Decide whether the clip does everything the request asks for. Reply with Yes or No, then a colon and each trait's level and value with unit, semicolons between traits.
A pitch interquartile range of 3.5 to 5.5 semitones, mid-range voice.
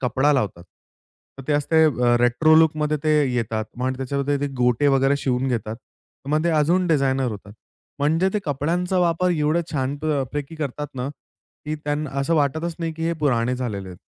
Yes: average, 3.8 semitones; medium, 145 Hz